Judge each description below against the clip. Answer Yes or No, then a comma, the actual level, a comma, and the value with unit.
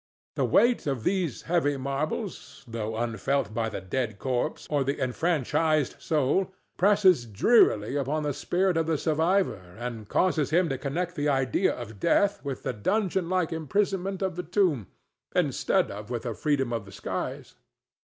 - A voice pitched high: No, medium, 145 Hz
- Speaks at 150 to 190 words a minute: Yes, average, 160 wpm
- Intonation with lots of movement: Yes, wide, 6.8 semitones